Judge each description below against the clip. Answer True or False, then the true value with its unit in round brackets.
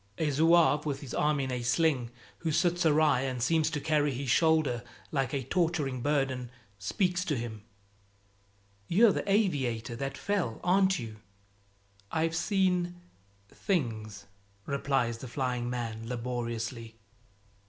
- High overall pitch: False (140 Hz)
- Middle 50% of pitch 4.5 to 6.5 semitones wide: True (5.3 semitones)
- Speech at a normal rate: False (130 wpm)